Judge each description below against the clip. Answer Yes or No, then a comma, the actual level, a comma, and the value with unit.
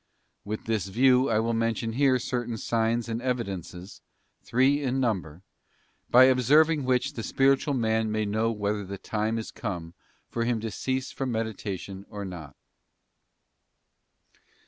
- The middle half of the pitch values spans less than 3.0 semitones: No, average, 3.6 semitones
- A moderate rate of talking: Yes, average, 145 wpm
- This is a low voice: Yes, low, 115 Hz